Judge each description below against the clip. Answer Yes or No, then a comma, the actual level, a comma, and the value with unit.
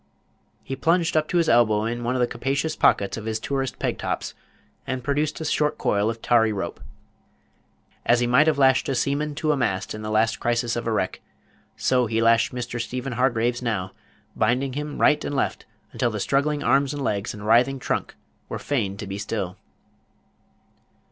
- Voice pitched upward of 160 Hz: No, low, 120 Hz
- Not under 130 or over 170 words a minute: No, average, 195 wpm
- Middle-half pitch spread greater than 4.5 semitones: No, average, 3.8 semitones